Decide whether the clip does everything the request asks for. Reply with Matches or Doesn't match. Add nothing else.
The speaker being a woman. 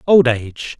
Doesn't match